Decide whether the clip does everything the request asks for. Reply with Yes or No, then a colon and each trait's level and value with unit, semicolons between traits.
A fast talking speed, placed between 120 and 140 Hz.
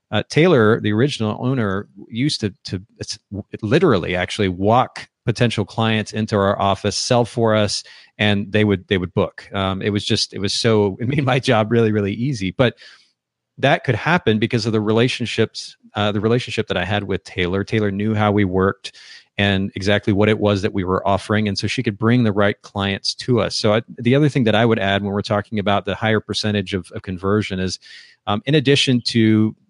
No: fast, 210 wpm; low, 105 Hz